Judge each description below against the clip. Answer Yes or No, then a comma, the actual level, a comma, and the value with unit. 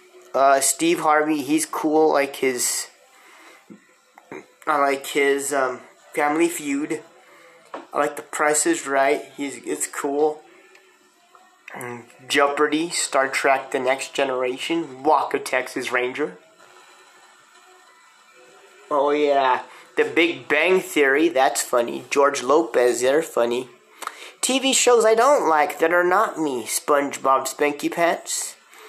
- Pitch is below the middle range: No, medium, 150 Hz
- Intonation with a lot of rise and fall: Yes, wide, 7.1 semitones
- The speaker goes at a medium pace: No, slow, 115 wpm